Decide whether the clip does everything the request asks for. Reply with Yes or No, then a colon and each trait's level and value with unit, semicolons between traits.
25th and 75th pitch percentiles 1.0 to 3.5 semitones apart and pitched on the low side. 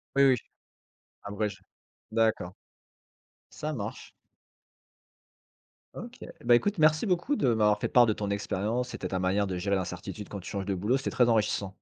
No: average, 4.0 semitones; low, 105 Hz